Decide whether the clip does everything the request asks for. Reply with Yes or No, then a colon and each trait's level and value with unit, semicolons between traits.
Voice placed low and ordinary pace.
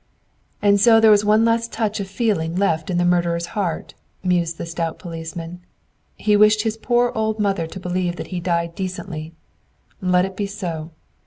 No: medium, 185 Hz; average, 180 wpm